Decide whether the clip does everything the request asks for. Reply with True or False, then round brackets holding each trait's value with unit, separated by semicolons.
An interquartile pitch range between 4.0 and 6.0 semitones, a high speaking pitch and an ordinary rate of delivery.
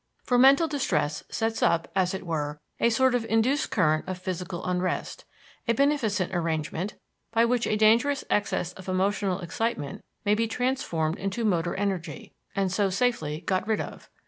True (4.7 semitones; 195 Hz; 165 wpm)